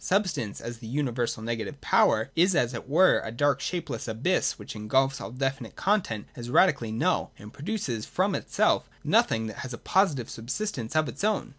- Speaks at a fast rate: No, average, 180 wpm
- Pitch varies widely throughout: Yes, wide, 6.0 semitones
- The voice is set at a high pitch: No, low, 130 Hz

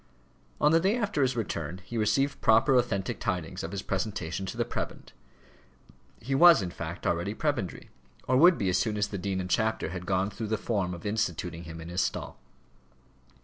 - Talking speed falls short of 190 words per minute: No, average, 195 wpm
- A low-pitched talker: Yes, low, 100 Hz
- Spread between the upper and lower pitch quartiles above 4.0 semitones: Yes, average, 5.2 semitones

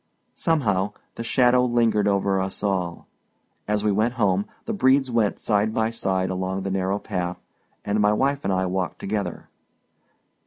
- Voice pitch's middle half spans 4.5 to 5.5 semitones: No, average, 3.4 semitones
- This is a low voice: Yes, low, 105 Hz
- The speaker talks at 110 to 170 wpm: Yes, average, 160 wpm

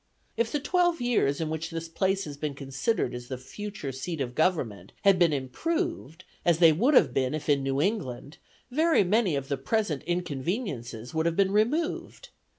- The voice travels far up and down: Yes, wide, 7.3 semitones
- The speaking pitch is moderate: Yes, medium, 165 Hz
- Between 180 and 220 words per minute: Yes, average, 185 wpm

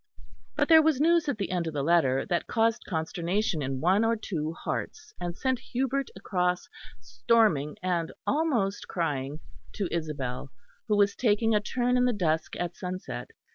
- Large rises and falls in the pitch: Yes, wide, 6.3 semitones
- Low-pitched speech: No, medium, 185 Hz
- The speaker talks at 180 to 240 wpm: No, average, 170 wpm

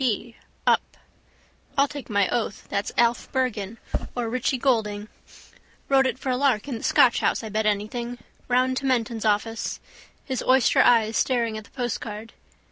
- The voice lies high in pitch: Yes, high, 235 Hz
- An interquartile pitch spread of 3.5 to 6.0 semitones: No, average, 2.9 semitones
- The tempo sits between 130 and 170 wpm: Yes, average, 165 wpm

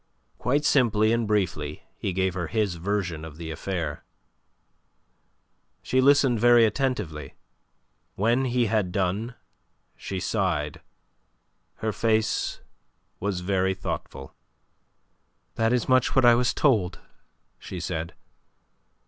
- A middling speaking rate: No, slow, 115 wpm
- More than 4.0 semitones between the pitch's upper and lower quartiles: Yes, average, 5.0 semitones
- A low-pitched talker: Yes, low, 100 Hz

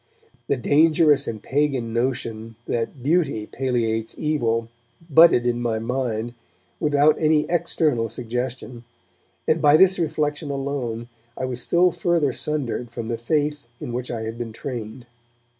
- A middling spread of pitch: Yes, average, 4.4 semitones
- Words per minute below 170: Yes, average, 140 wpm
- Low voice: Yes, low, 130 Hz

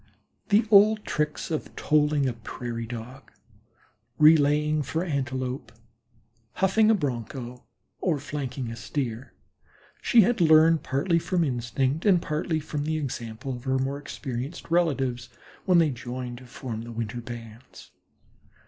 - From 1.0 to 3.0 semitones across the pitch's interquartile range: No, average, 4.6 semitones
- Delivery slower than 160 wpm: Yes, slow, 135 wpm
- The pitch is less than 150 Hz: Yes, medium, 140 Hz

